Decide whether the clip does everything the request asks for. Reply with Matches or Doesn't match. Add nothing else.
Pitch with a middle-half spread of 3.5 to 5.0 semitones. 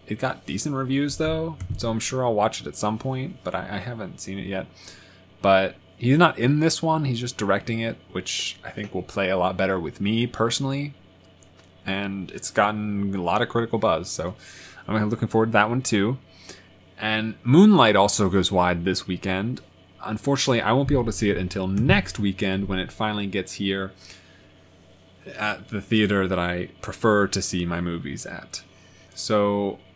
Matches